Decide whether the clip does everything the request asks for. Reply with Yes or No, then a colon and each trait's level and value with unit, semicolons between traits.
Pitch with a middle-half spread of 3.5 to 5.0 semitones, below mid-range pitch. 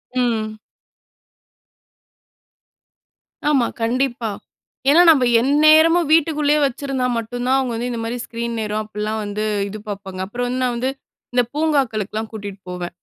No: average, 4.1 semitones; high, 240 Hz